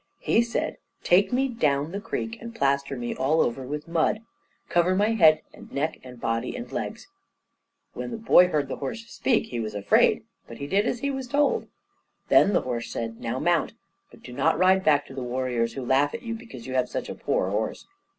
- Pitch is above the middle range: No, medium, 150 Hz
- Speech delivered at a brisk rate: Yes, fast, 215 wpm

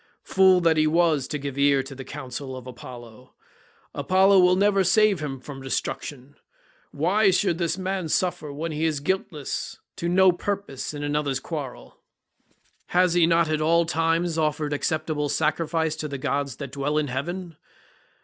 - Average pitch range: Yes, average, 3.7 semitones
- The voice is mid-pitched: Yes, medium, 155 Hz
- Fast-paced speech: No, average, 170 wpm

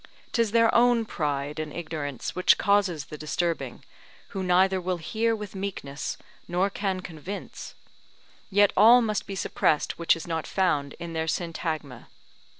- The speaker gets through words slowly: No, average, 150 wpm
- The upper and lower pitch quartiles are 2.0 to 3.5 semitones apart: No, average, 4.4 semitones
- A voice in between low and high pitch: Yes, medium, 180 Hz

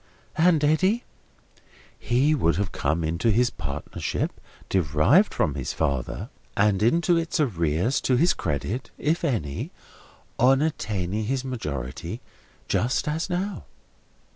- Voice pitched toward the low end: Yes, low, 115 Hz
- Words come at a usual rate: No, slow, 120 wpm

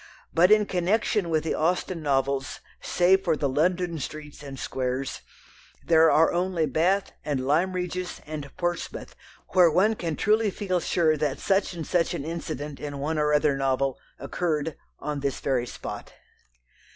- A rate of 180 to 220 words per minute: No, average, 160 wpm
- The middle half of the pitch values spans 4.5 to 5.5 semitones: No, average, 3.9 semitones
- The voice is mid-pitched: Yes, medium, 160 Hz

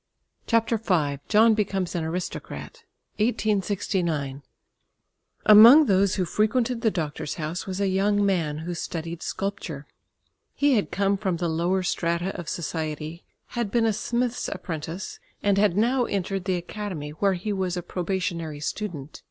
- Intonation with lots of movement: No, average, 3.9 semitones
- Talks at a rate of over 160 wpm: No, average, 145 wpm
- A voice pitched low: No, high, 190 Hz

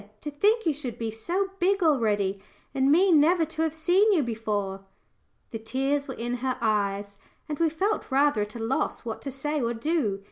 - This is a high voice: Yes, very high, 270 Hz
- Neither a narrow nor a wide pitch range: No, wide, 6.4 semitones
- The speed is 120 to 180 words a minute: No, average, 200 wpm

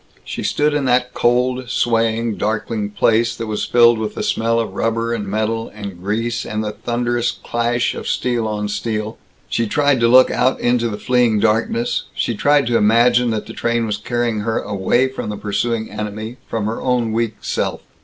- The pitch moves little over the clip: Yes, narrow, 2.0 semitones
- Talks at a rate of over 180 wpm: Yes, average, 190 wpm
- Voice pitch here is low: Yes, low, 115 Hz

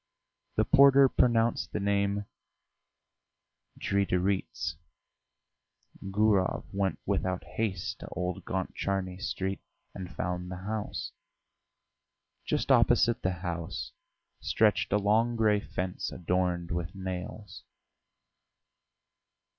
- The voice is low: Yes, very low, 95 Hz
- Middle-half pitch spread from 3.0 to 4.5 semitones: No, narrow, 2.4 semitones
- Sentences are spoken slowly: Yes, slow, 90 wpm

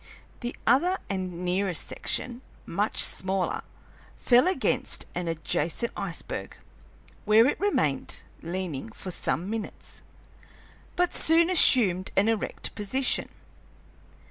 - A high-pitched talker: Yes, high, 205 Hz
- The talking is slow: Yes, slow, 105 wpm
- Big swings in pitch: Yes, wide, 5.8 semitones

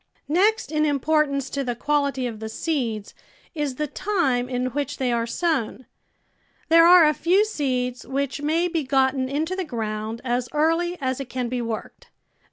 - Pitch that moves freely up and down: No, average, 4.1 semitones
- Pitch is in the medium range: No, very high, 275 Hz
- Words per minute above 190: No, average, 175 wpm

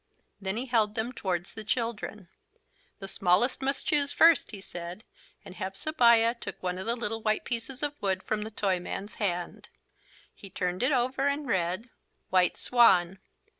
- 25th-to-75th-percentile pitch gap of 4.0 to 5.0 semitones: Yes, average, 4.5 semitones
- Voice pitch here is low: No, high, 215 Hz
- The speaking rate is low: No, average, 165 wpm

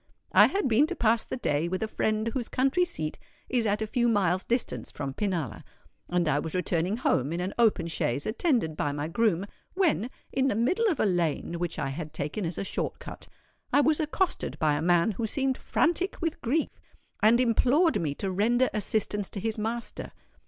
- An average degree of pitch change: No, wide, 6.9 semitones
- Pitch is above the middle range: Yes, high, 215 Hz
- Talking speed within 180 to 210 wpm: Yes, average, 200 wpm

